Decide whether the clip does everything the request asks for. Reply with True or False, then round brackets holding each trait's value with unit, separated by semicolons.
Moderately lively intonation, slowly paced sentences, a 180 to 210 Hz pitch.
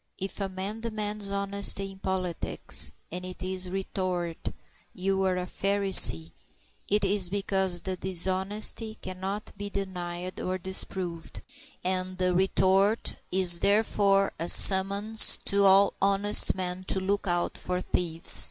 False (1.5 semitones; 130 wpm; 190 Hz)